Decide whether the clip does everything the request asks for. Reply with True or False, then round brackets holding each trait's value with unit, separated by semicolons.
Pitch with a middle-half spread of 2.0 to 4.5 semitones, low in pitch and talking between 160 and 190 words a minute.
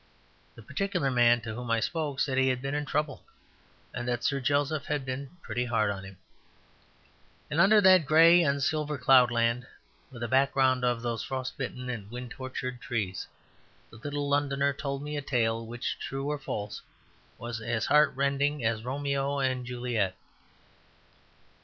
True (3.1 semitones; 130 Hz; 165 wpm)